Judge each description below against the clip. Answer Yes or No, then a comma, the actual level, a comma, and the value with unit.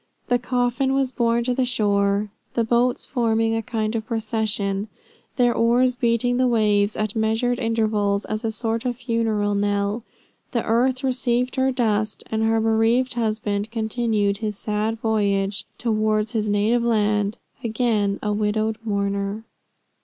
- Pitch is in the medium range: No, high, 225 Hz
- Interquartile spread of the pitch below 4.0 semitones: Yes, narrow, 2.4 semitones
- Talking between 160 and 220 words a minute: No, average, 145 wpm